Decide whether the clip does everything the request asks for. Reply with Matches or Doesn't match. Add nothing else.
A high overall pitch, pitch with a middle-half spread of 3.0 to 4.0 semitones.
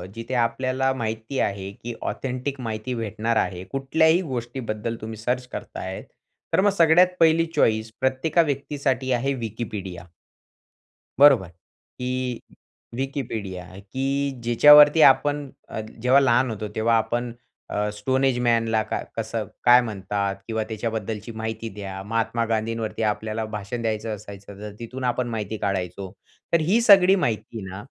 Doesn't match